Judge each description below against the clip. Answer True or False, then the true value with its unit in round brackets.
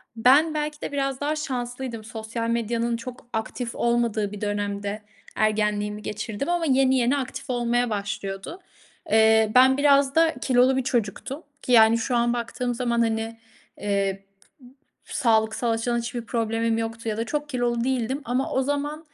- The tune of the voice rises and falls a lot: False (3.0 semitones)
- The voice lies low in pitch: False (235 Hz)